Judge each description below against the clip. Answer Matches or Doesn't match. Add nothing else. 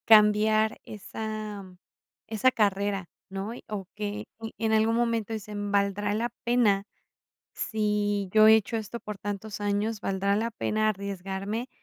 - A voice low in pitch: Doesn't match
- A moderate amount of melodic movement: Doesn't match